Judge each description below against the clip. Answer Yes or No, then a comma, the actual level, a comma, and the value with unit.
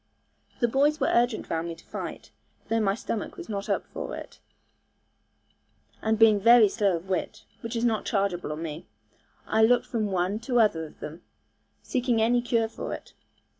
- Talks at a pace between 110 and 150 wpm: No, average, 180 wpm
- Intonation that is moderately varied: Yes, average, 3.8 semitones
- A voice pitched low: No, high, 220 Hz